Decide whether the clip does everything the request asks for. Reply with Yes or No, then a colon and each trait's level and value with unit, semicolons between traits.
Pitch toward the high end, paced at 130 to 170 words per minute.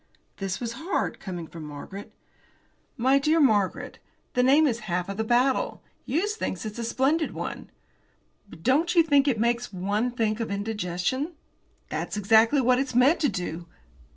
Yes: high, 235 Hz; average, 165 wpm